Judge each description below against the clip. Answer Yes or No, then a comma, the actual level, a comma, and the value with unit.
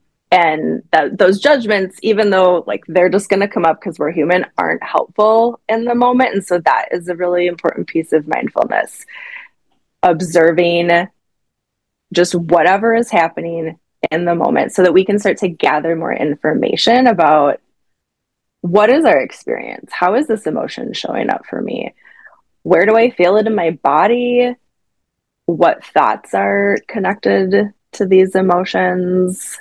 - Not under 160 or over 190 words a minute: No, average, 150 wpm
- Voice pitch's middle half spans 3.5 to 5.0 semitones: Yes, average, 4.2 semitones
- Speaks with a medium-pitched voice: Yes, medium, 180 Hz